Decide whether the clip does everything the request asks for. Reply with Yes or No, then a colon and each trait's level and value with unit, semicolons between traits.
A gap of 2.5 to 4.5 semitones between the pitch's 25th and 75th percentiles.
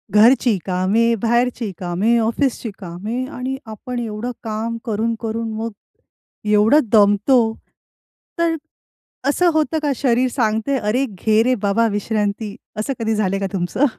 Yes: average, 3.0 semitones